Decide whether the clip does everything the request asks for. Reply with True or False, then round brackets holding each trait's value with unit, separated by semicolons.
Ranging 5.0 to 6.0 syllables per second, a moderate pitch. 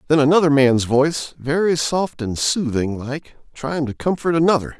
False (4.7 syllables/s; 145 Hz)